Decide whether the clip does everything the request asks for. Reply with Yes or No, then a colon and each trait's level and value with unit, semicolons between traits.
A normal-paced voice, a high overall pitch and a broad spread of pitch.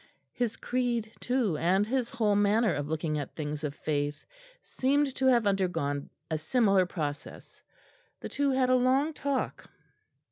Yes: average, 150 wpm; high, 210 Hz; wide, 8.6 semitones